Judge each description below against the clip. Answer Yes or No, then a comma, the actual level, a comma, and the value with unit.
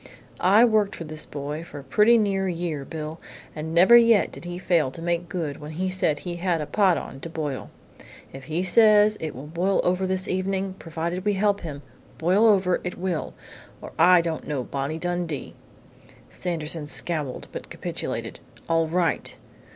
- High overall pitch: No, medium, 175 Hz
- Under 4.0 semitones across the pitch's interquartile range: Yes, average, 3.3 semitones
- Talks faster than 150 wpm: Yes, average, 180 wpm